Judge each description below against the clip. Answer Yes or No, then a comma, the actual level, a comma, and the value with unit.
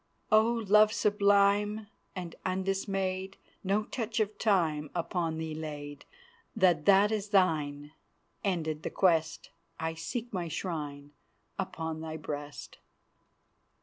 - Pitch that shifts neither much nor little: Yes, average, 4.3 semitones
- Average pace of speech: No, slow, 115 wpm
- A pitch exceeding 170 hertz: Yes, medium, 185 Hz